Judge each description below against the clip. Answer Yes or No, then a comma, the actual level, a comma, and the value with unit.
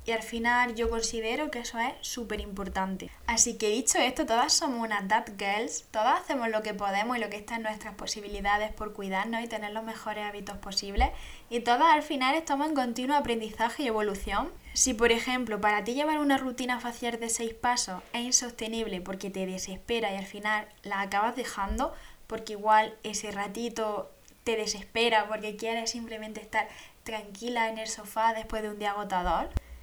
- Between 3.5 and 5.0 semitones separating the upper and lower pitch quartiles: No, narrow, 2.4 semitones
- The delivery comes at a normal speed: Yes, average, 180 wpm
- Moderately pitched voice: No, high, 220 Hz